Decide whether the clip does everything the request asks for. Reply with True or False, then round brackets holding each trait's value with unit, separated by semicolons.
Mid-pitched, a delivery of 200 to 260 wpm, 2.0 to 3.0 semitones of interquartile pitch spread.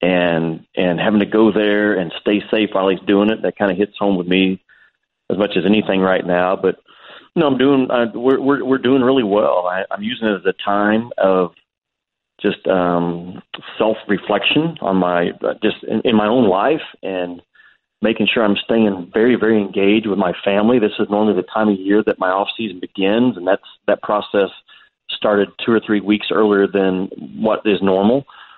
False (105 Hz; 205 wpm; 2.6 semitones)